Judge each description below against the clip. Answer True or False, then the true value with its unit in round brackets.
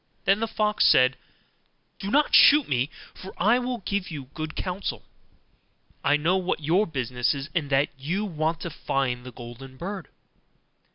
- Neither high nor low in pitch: True (160 Hz)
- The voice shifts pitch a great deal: True (6.6 semitones)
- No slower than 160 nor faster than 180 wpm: True (165 wpm)